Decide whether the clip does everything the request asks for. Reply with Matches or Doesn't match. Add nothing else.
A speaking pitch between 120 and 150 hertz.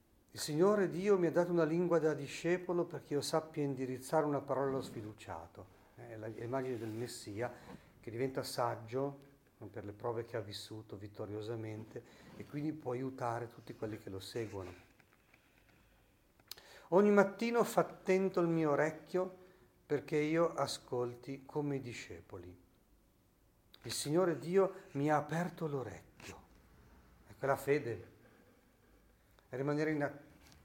Matches